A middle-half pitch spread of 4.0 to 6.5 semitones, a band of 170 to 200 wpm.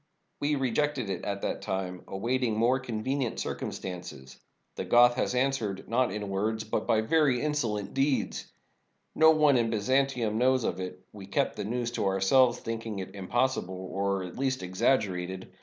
Yes: average, 5.1 semitones; average, 175 wpm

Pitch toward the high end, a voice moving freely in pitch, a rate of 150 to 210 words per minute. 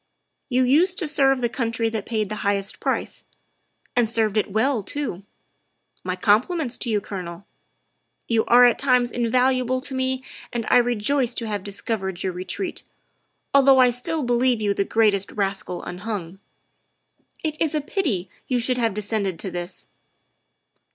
No: high, 230 Hz; average, 4.2 semitones; average, 160 wpm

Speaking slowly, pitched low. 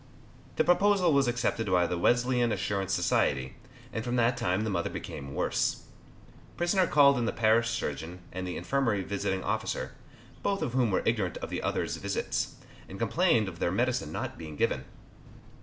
No: average, 175 wpm; low, 110 Hz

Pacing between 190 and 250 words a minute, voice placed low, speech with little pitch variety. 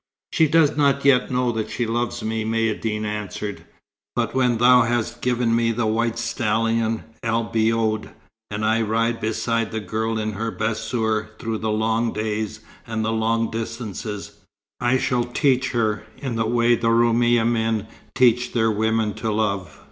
No: average, 165 wpm; low, 115 Hz; narrow, 1.5 semitones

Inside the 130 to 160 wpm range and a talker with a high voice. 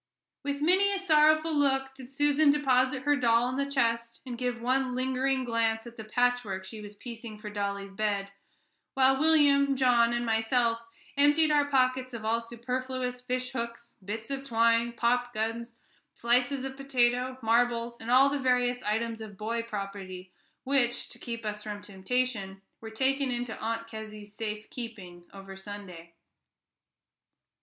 Yes: average, 155 wpm; high, 240 Hz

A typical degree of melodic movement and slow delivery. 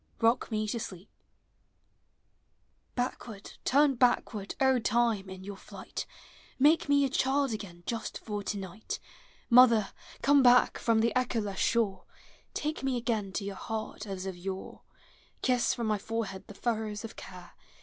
No: average, 3.8 semitones; average, 150 wpm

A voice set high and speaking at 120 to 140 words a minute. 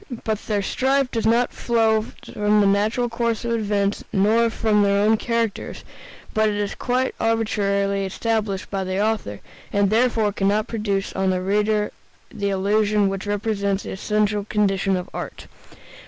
No: high, 210 Hz; average, 155 wpm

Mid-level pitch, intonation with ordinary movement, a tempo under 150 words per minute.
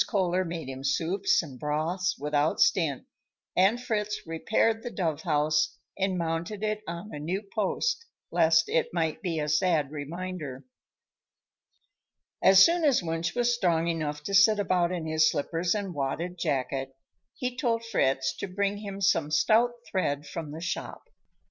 No: medium, 170 Hz; average, 4.6 semitones; average, 155 wpm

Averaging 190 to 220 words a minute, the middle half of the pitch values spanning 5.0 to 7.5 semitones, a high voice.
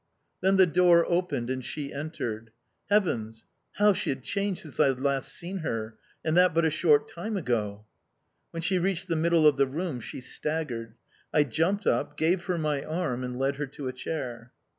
No: average, 195 wpm; wide, 5.5 semitones; medium, 155 Hz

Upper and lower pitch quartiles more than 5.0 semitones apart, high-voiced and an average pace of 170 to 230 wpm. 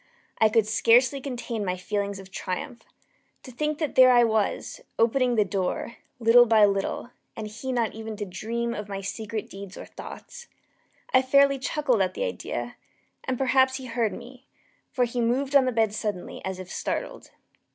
No: average, 3.6 semitones; high, 230 Hz; average, 180 wpm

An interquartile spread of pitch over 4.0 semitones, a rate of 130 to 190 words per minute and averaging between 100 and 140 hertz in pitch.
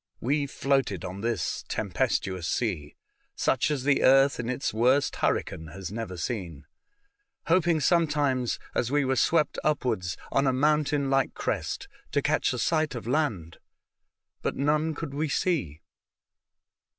Yes: average, 5.1 semitones; average, 150 wpm; low, 135 Hz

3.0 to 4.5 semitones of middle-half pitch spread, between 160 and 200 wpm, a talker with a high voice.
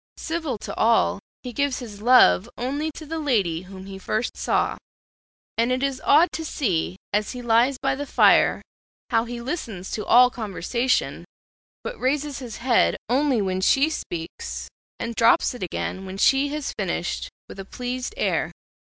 No: average, 5.2 semitones; average, 170 wpm; high, 245 Hz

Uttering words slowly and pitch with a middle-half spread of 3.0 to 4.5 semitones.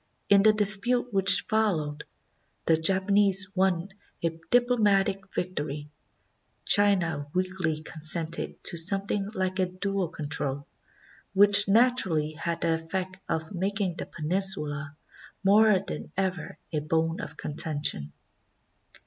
Yes: slow, 120 wpm; average, 3.8 semitones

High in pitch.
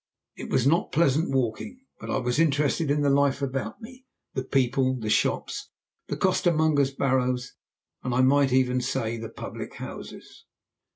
No: low, 135 Hz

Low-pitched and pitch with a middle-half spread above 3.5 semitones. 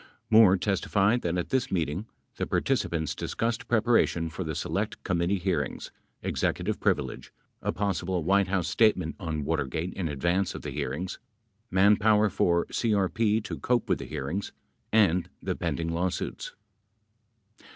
Yes: very low, 95 Hz; average, 4.1 semitones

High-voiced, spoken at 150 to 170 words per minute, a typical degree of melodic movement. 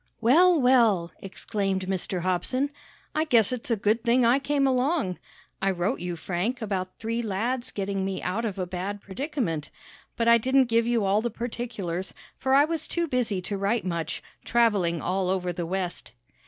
No: high, 215 Hz; average, 180 wpm; average, 5.0 semitones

